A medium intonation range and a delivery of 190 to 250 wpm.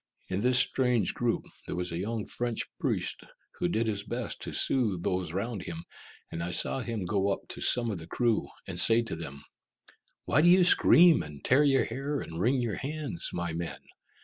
No: wide, 6.0 semitones; average, 200 wpm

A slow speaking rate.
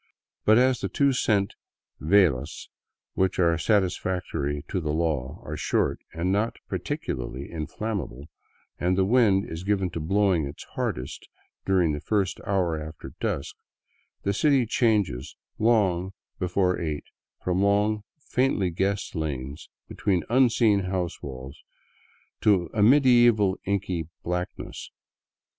Yes: slow, 125 wpm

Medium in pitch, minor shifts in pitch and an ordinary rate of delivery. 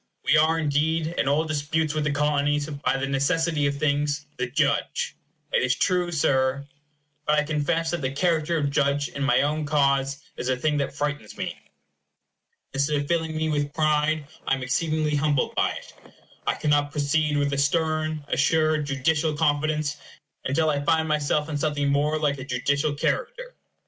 Yes: medium, 150 Hz; narrow, 1.7 semitones; average, 175 wpm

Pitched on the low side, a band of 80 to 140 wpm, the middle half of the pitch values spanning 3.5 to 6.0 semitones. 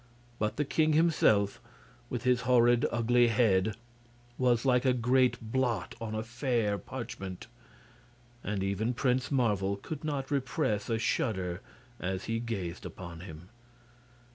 Yes: low, 115 Hz; slow, 135 wpm; average, 4.0 semitones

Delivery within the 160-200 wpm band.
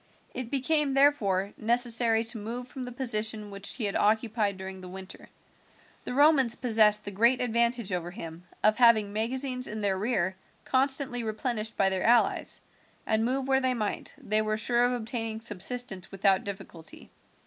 Yes: average, 165 wpm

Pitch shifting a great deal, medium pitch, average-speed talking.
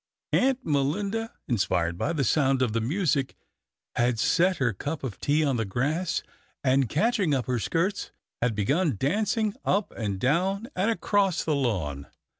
Yes: wide, 7.7 semitones; medium, 145 Hz; average, 160 wpm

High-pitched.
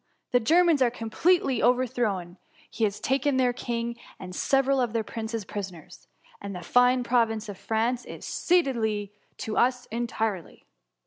Yes: high, 235 Hz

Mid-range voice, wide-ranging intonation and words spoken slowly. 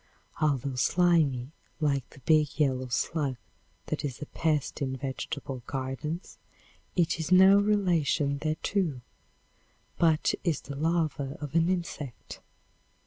No: medium, 150 Hz; average, 3.7 semitones; slow, 120 wpm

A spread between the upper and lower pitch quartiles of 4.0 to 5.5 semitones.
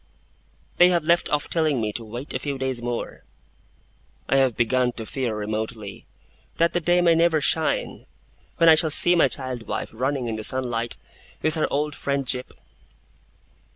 Yes: average, 4.9 semitones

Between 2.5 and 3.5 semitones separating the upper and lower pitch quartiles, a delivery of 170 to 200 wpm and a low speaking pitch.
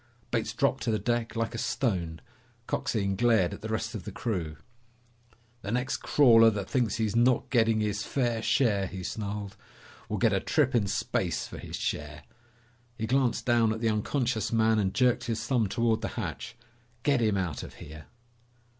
Yes: average, 3.0 semitones; average, 180 wpm; low, 110 Hz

